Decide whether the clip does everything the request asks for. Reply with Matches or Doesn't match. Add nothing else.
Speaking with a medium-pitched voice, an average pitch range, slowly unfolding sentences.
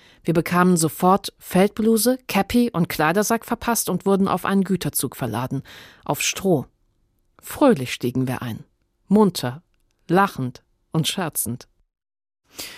Doesn't match